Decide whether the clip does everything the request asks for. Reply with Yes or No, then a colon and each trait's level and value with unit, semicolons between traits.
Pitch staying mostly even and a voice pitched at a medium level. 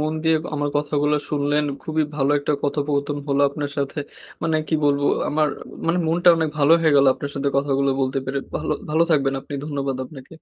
Yes: narrow, 1.6 semitones; medium, 145 Hz